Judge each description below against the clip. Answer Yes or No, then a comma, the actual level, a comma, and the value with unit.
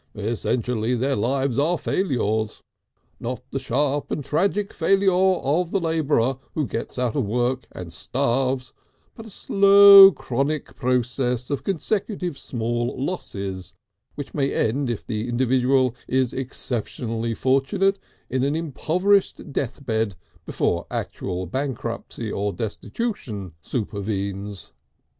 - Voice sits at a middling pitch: No, low, 130 Hz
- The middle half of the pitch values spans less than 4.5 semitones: No, wide, 5.5 semitones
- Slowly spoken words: Yes, slow, 120 wpm